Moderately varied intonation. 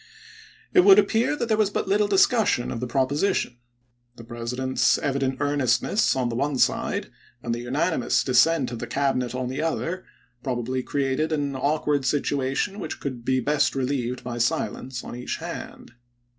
Yes: average, 3.9 semitones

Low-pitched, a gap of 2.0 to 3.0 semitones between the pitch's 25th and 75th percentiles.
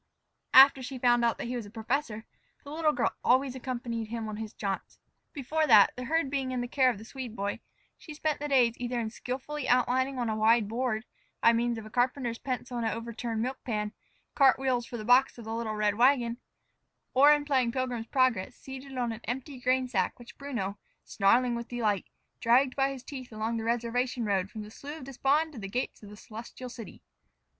No: high, 245 Hz; average, 2.7 semitones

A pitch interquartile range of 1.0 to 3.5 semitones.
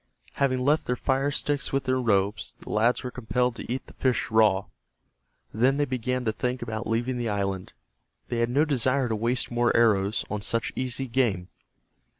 Yes: average, 2.7 semitones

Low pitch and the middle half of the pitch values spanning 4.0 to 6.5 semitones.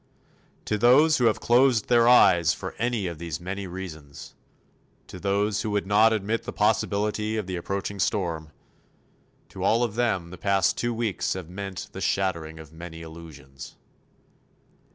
Yes: low, 100 Hz; average, 4.4 semitones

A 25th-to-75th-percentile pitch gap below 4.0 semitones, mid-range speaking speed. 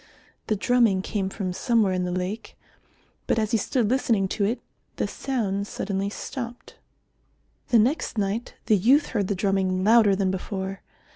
Yes: average, 3.3 semitones; average, 160 wpm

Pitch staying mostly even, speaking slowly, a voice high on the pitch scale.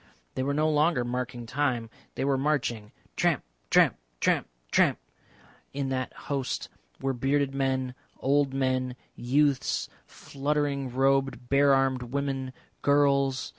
No: narrow, 1.7 semitones; slow, 125 wpm; low, 135 Hz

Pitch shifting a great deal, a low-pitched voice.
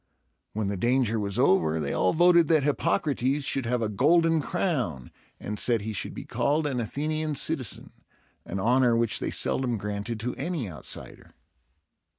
Yes: wide, 6.0 semitones; low, 125 Hz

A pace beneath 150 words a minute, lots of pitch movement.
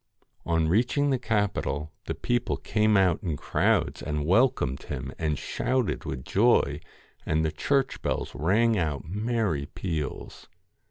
Yes: average, 140 wpm; wide, 7.3 semitones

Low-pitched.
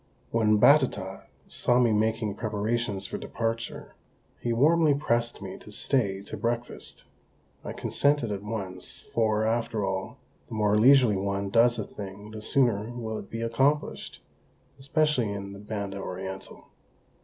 Yes: low, 110 Hz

